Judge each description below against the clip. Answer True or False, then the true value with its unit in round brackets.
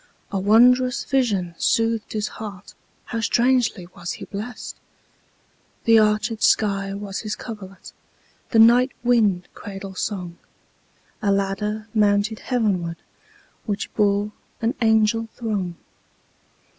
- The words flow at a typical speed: False (95 wpm)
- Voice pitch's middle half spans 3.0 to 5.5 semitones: False (2.5 semitones)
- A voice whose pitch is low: False (210 Hz)